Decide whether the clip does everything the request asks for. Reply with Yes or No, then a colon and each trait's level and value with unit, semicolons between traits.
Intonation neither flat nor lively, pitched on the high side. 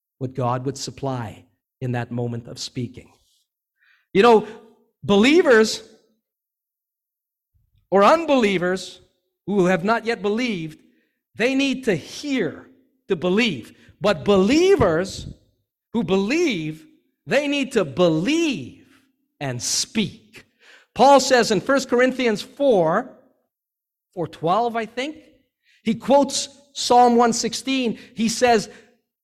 No: wide, 6.5 semitones; high, 225 Hz